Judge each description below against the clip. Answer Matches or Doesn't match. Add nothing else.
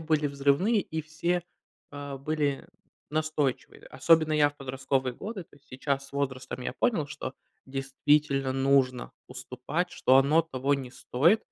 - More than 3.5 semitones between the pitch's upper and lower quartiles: Doesn't match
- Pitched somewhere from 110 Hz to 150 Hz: Matches